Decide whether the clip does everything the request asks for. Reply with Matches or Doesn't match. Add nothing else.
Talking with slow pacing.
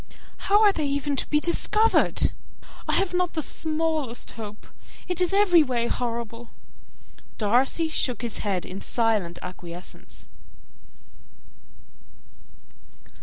Matches